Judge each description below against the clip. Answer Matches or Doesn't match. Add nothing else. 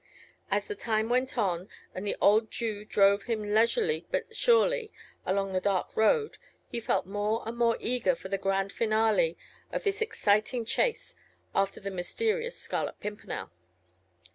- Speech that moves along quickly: Doesn't match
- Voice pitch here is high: Matches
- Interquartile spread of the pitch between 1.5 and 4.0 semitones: Doesn't match